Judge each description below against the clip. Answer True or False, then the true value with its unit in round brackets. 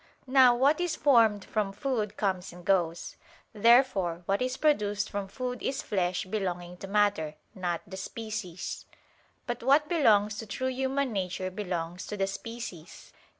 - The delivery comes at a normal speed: True (155 wpm)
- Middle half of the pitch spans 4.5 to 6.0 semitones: True (5.1 semitones)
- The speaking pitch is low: False (205 Hz)